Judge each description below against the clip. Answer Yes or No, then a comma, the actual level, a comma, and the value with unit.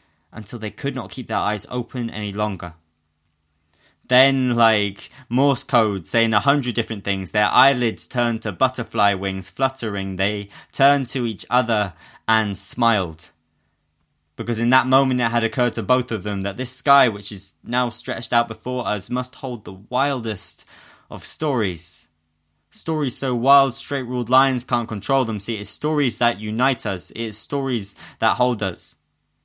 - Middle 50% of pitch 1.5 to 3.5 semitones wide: No, average, 4.1 semitones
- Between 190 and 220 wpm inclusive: No, average, 165 wpm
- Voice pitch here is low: Yes, low, 115 Hz